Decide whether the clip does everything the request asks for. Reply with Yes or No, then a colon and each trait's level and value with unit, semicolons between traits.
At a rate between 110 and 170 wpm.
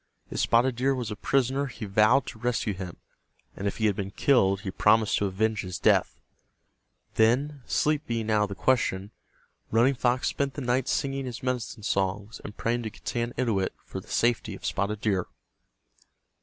No: average, 180 wpm